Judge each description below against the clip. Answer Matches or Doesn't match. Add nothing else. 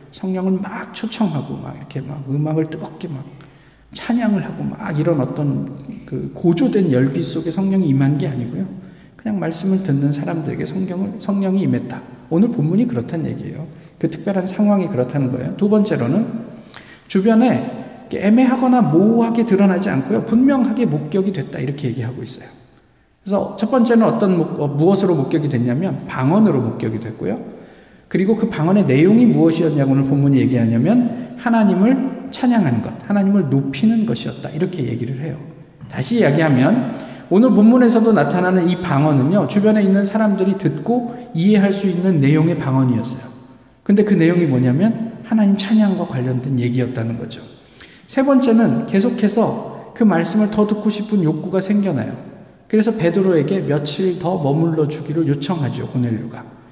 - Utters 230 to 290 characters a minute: Doesn't match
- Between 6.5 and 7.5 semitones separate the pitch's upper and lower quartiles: Matches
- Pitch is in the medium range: Matches